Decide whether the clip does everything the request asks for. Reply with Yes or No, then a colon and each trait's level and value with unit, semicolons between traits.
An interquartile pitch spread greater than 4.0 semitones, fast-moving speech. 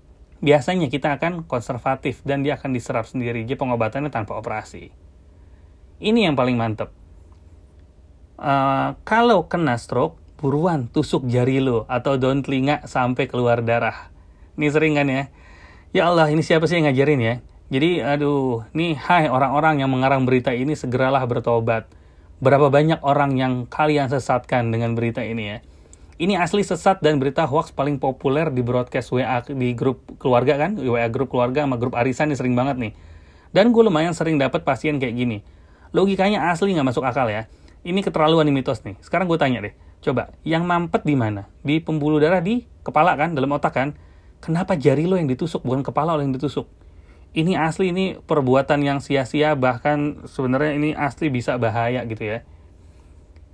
Yes: average, 4.8 semitones; fast, 170 wpm